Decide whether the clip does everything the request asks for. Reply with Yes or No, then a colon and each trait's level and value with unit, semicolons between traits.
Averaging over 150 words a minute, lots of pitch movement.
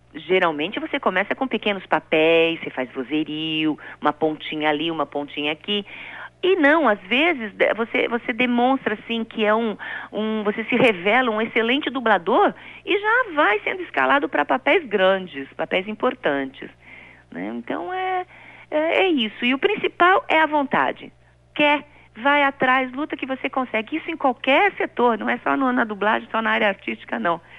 Yes: average, 165 wpm; wide, 7.7 semitones